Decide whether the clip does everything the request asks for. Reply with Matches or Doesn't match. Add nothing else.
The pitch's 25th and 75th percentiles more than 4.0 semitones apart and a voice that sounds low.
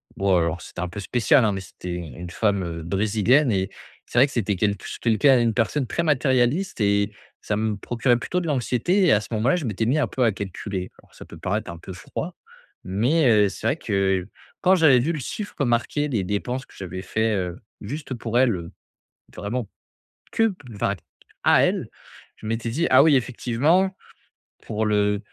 Matches